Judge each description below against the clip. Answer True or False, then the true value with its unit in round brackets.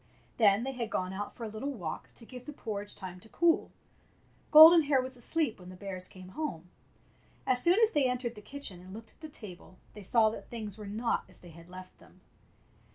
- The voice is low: False (220 Hz)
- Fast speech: True (225 wpm)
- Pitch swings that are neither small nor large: False (5.8 semitones)